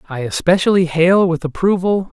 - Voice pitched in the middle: Yes, medium, 175 Hz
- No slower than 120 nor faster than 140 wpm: Yes, slow, 135 wpm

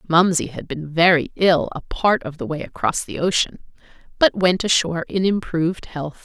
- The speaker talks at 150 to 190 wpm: Yes, average, 185 wpm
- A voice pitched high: No, medium, 170 Hz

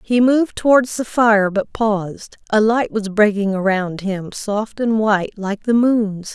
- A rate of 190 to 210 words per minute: No, average, 180 wpm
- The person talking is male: No, female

